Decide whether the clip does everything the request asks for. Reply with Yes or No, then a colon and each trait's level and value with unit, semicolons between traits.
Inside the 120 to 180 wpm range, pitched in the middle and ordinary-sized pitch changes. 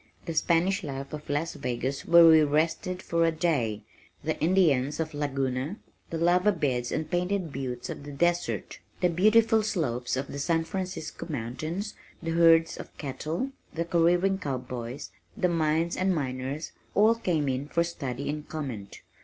Yes: average, 160 wpm; medium, 160 Hz; average, 4.2 semitones